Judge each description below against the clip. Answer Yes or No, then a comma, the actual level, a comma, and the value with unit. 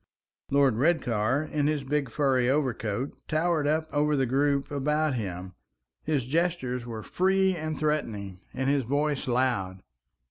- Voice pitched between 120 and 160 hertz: Yes, medium, 140 Hz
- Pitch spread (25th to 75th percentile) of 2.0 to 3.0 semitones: No, average, 3.8 semitones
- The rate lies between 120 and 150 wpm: Yes, average, 140 wpm